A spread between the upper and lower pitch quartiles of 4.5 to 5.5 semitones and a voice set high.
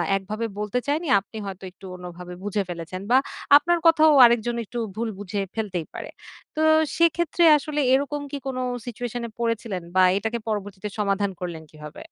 Yes: average, 5.1 semitones; high, 215 Hz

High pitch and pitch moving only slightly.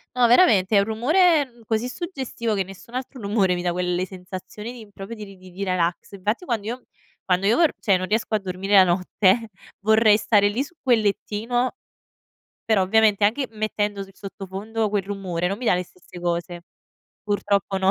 No: high, 205 Hz; average, 3.2 semitones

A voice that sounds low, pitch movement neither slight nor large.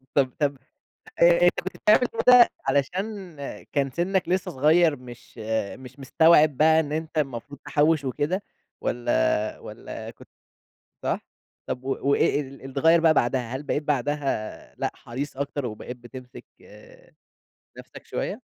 No: medium, 145 Hz; average, 3.9 semitones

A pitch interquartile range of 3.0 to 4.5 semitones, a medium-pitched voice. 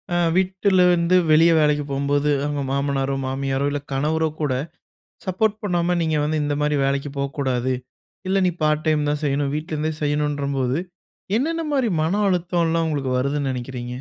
Yes: average, 3.4 semitones; medium, 150 Hz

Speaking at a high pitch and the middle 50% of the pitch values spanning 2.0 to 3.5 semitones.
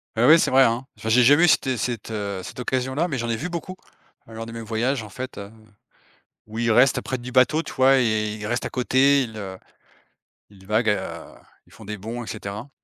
No: low, 120 Hz; average, 3.2 semitones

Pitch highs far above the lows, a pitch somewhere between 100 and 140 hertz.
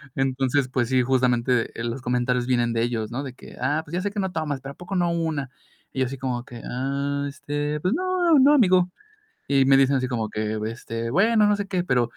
Yes: wide, 5.8 semitones; low, 135 Hz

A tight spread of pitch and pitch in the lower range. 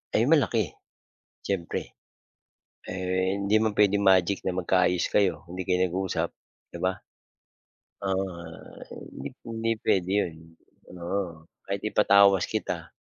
Yes: narrow, 2.0 semitones; very low, 95 Hz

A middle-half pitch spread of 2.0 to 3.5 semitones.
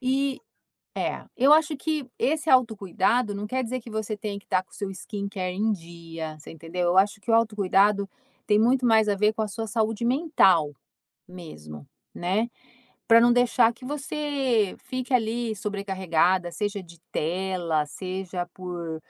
No: average, 4.6 semitones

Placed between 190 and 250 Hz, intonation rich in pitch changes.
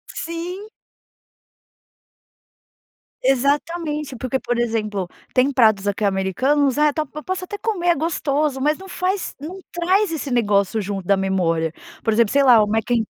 No: very high, 270 Hz; wide, 7.5 semitones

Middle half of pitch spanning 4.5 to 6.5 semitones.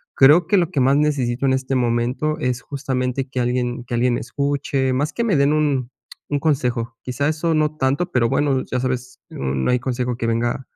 No: average, 2.8 semitones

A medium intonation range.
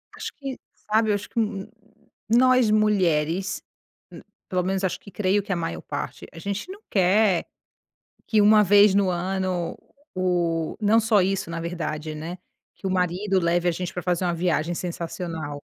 Yes: average, 3.2 semitones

